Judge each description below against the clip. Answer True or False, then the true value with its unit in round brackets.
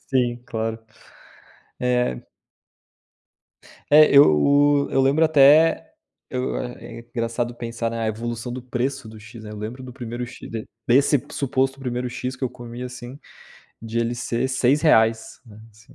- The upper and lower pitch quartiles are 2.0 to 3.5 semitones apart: True (2.4 semitones)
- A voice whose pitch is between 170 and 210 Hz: False (120 Hz)